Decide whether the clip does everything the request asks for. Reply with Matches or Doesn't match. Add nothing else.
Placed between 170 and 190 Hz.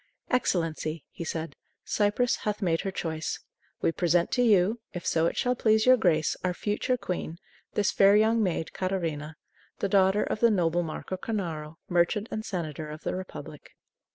Matches